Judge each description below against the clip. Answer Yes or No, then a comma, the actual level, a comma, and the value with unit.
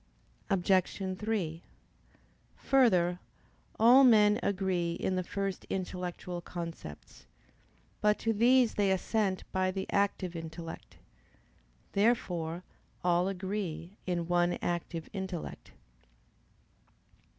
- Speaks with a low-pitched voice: No, medium, 185 Hz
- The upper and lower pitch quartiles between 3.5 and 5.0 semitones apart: No, average, 2.8 semitones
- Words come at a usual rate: No, slow, 95 wpm